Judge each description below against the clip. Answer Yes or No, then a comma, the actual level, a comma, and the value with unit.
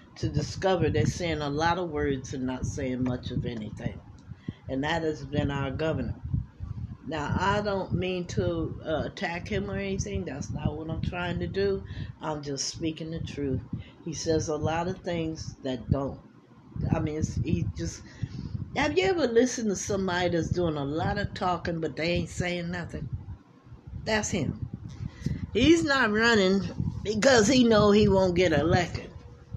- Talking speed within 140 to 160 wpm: No, average, 170 wpm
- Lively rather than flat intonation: Yes, wide, 5.7 semitones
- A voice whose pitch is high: No, medium, 155 Hz